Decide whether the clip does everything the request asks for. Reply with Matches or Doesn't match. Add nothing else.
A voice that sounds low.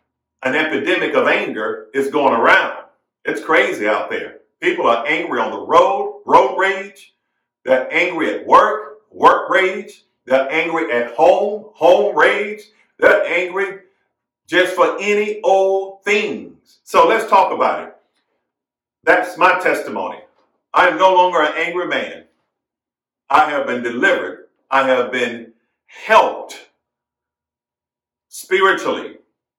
Doesn't match